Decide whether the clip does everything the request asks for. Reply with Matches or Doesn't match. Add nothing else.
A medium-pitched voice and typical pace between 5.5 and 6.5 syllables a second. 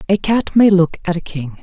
Doesn't match